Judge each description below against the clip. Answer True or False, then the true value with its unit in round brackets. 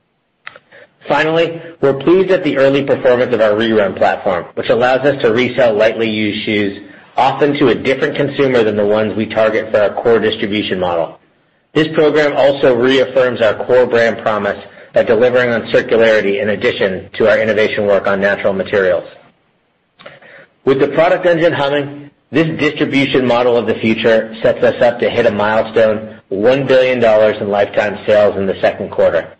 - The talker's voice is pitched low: True (125 Hz)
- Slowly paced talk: False (165 wpm)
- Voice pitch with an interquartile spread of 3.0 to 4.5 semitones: False (4.9 semitones)